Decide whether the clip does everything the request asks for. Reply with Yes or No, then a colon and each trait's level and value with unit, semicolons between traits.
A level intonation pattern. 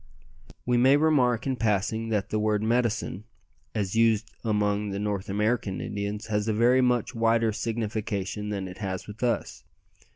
Yes: narrow, 2.1 semitones